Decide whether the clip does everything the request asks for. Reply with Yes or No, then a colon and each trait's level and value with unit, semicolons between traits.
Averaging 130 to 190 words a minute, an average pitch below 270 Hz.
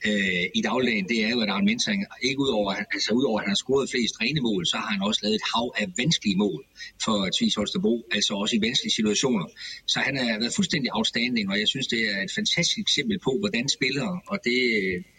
No: average, 220 wpm; high, 190 Hz